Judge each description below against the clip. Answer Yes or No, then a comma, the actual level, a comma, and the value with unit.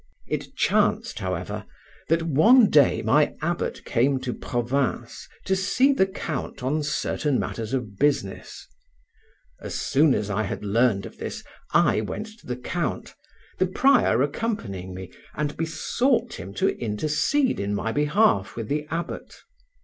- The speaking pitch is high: No, medium, 140 Hz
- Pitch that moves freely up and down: Yes, wide, 8.3 semitones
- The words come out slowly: No, average, 145 wpm